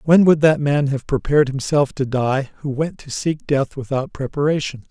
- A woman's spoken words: No, male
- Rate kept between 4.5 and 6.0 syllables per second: Yes, 5.0 syllables/s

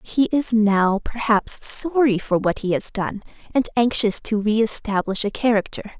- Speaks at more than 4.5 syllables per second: No, 4.4 syllables/s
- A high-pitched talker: Yes, high, 220 Hz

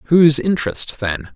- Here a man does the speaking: Yes, male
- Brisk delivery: No, slow, 130 wpm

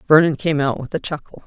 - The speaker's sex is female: Yes, female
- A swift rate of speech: Yes, fast, 245 wpm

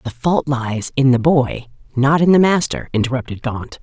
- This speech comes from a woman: Yes, female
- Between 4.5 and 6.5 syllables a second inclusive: Yes, 4.8 syllables/s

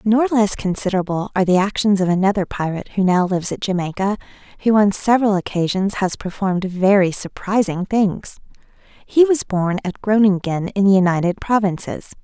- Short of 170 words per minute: Yes, average, 155 wpm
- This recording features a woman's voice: Yes, female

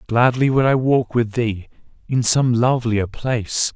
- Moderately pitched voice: No, low, 120 Hz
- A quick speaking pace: No, average, 145 wpm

